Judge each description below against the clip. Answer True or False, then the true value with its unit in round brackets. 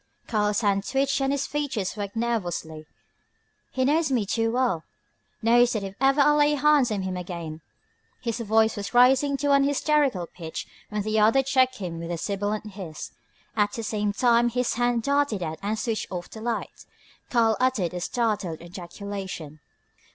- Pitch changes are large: False (5.0 semitones)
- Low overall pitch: False (220 Hz)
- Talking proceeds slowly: False (175 wpm)